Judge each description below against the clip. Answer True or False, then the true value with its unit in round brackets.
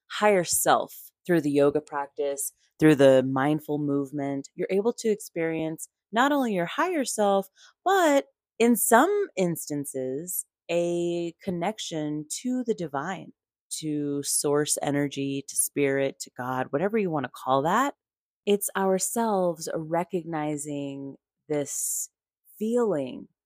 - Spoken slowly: True (120 wpm)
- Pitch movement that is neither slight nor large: False (6.3 semitones)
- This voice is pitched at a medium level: True (165 Hz)